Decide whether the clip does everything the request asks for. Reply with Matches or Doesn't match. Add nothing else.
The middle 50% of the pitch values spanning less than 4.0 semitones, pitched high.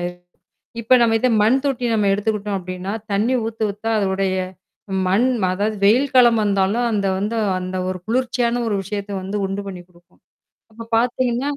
Matches